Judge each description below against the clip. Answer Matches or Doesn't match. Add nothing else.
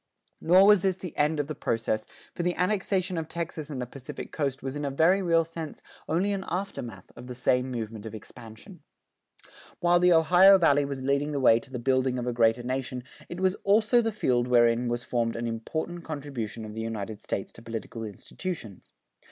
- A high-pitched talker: Doesn't match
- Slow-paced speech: Doesn't match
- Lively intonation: Matches